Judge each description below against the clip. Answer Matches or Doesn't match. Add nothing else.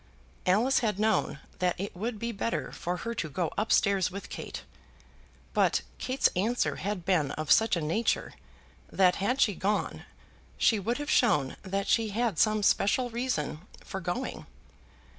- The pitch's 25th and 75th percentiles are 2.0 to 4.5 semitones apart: Matches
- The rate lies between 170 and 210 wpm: Doesn't match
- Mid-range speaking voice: Doesn't match